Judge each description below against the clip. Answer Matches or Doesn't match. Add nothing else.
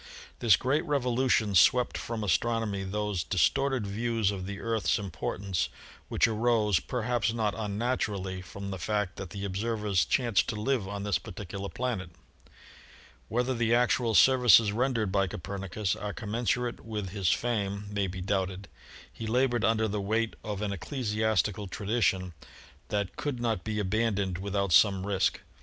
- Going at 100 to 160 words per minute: Matches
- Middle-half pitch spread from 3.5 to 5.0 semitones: Doesn't match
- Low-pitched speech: Matches